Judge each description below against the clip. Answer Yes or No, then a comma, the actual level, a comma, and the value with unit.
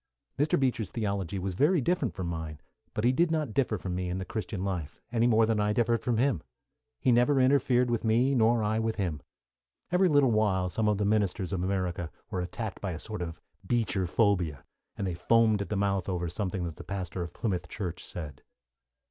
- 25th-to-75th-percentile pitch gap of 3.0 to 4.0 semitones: No, average, 4.6 semitones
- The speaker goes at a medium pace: No, fast, 210 wpm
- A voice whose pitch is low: Yes, low, 105 Hz